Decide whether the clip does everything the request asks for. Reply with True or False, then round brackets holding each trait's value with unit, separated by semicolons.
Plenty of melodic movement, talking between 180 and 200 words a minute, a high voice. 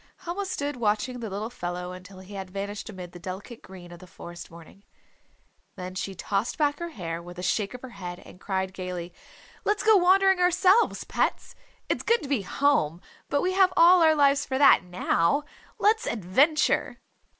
True (8.8 semitones; 185 wpm; 210 Hz)